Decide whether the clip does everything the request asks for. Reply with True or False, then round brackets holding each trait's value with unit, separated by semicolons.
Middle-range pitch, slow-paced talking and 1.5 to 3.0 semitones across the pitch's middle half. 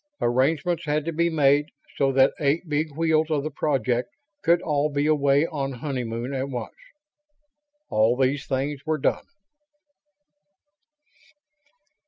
True (145 Hz; 130 wpm; 2.5 semitones)